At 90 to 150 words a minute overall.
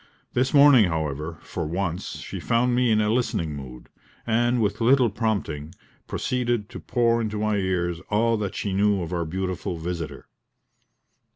No: average, 160 wpm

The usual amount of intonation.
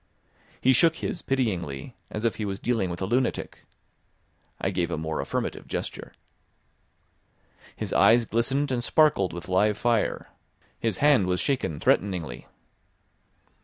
No: wide, 5.7 semitones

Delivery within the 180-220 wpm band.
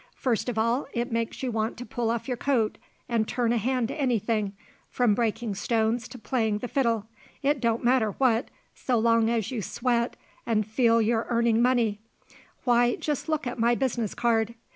Yes: average, 195 wpm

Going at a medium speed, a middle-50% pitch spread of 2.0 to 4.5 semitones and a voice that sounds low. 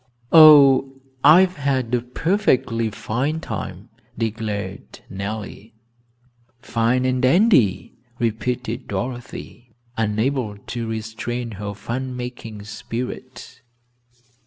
No: slow, 85 wpm; average, 2.9 semitones; low, 120 Hz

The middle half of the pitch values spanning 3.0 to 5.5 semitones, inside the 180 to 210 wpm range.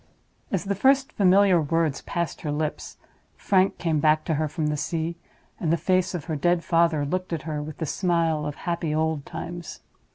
No: narrow, 2.5 semitones; average, 195 wpm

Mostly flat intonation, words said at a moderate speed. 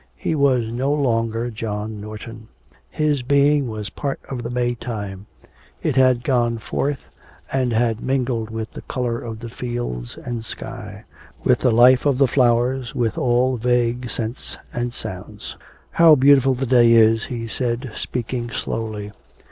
Yes: narrow, 2.3 semitones; average, 155 wpm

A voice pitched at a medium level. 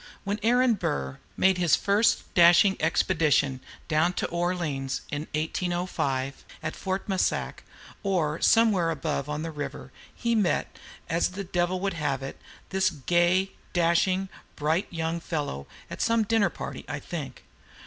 Yes: medium, 170 Hz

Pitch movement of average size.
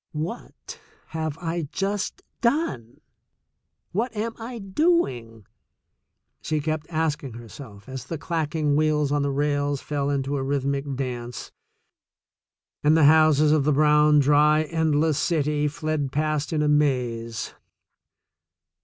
No: narrow, 2.3 semitones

